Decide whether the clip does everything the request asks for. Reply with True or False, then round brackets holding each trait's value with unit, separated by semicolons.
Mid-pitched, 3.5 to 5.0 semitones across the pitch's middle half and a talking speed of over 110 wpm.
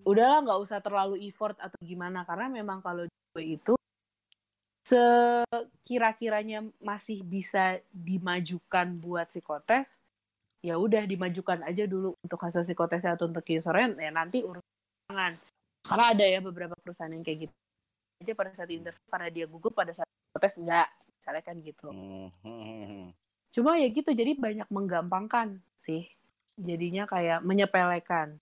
True (180 Hz; 4.0 semitones; 135 wpm)